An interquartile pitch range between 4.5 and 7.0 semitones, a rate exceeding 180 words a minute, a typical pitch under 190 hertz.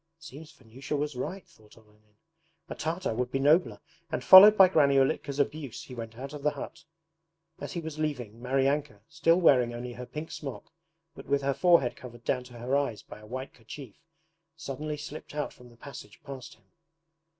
No: average, 3.6 semitones; average, 195 wpm; low, 135 Hz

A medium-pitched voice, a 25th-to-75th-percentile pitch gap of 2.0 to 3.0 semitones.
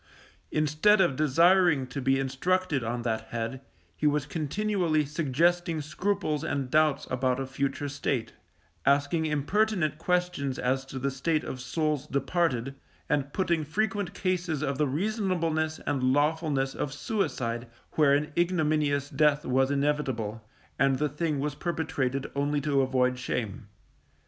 No: medium, 145 Hz; average, 3.4 semitones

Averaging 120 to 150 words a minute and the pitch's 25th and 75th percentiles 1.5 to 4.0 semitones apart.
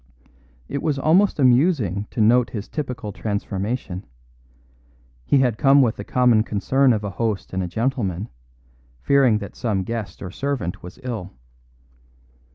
No: average, 145 wpm; average, 4.6 semitones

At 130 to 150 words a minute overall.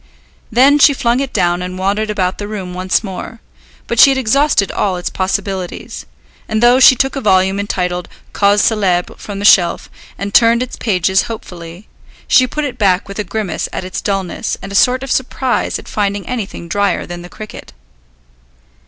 No: average, 185 wpm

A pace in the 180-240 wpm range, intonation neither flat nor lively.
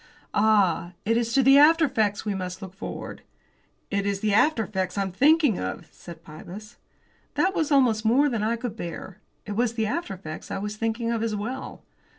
Yes: average, 195 wpm; average, 3.8 semitones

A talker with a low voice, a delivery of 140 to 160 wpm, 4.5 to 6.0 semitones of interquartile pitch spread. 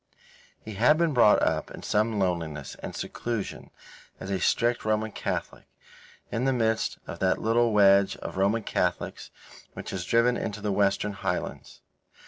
No: low, 105 Hz; average, 155 wpm; average, 3.2 semitones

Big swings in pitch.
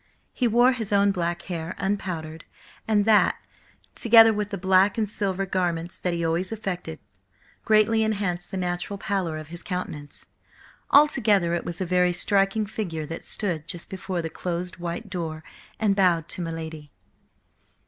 No: average, 3.3 semitones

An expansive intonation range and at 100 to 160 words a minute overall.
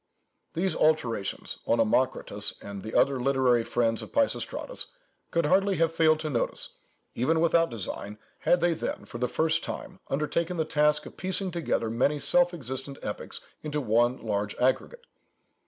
Yes: wide, 5.9 semitones; average, 155 wpm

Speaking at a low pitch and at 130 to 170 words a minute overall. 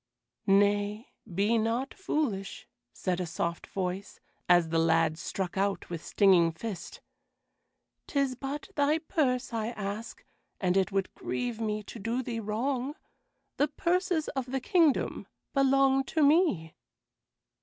No: high, 225 Hz; slow, 135 wpm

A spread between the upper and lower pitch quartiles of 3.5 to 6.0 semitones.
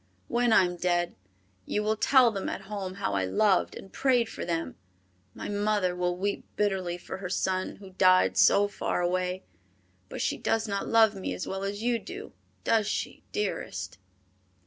No: average, 2.8 semitones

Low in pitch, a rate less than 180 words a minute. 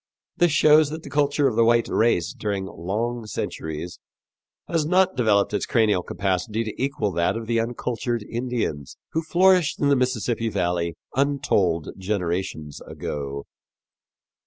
Yes: low, 115 Hz; average, 140 wpm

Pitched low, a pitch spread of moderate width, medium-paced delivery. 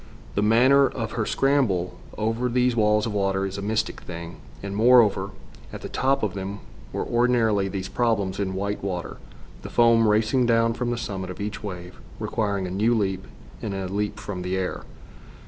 Yes: low, 105 Hz; average, 3.2 semitones; average, 185 wpm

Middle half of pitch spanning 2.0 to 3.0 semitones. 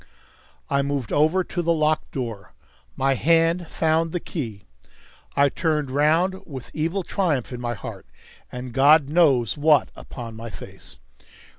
No: average, 4.2 semitones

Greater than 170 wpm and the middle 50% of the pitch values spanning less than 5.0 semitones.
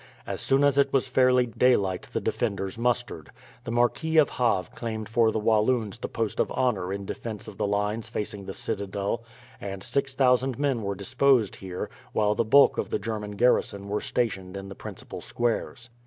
Yes: average, 185 wpm; average, 3.8 semitones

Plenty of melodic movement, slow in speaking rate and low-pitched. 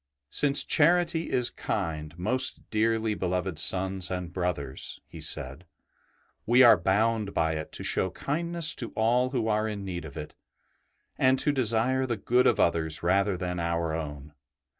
No: wide, 6.5 semitones; average, 165 wpm; low, 100 Hz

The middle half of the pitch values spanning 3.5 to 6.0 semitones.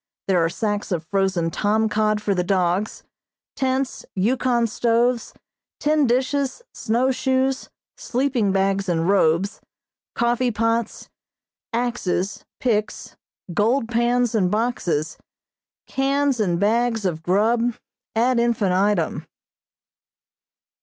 Yes: average, 4.0 semitones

